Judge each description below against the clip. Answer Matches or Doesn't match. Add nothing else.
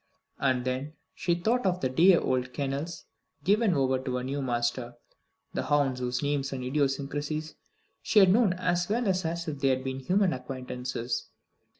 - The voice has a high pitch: Doesn't match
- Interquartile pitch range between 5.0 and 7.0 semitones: Matches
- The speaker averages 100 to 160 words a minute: Doesn't match